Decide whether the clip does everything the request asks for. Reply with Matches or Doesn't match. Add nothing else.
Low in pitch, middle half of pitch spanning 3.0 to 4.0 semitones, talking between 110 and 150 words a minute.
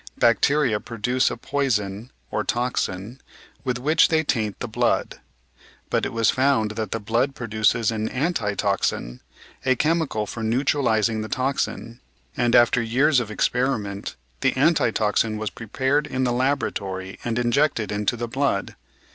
Matches